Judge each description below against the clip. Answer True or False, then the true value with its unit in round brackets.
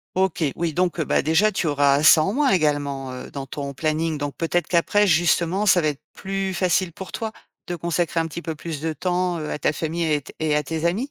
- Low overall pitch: False (165 Hz)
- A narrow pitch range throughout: False (3.3 semitones)